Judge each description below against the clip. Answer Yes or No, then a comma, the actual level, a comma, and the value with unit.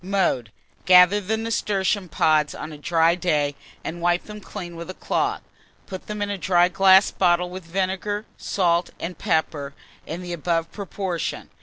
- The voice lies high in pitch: No, medium, 180 Hz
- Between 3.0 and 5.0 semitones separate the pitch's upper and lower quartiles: No, narrow, 2.5 semitones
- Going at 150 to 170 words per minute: Yes, average, 165 wpm